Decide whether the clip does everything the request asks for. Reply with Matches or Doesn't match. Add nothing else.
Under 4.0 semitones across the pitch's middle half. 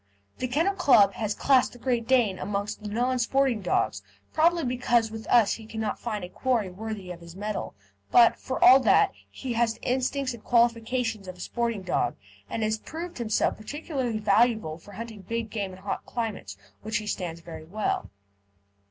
Matches